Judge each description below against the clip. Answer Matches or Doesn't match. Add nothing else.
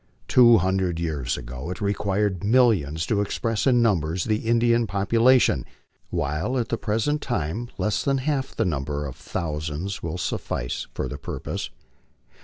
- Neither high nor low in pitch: Doesn't match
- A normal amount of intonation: Doesn't match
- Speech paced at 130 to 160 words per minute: Matches